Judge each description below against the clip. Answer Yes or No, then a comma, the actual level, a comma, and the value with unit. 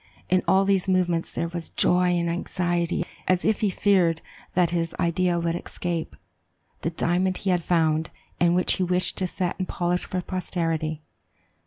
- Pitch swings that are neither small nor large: No, narrow, 1.6 semitones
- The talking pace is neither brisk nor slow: Yes, average, 170 wpm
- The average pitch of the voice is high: No, medium, 175 Hz